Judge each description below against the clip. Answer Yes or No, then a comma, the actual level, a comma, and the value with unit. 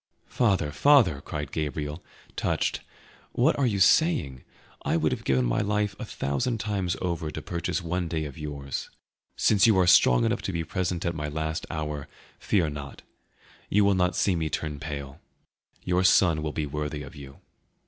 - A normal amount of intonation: Yes, average, 4.3 semitones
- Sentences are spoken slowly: No, average, 180 wpm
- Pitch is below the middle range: Yes, very low, 80 Hz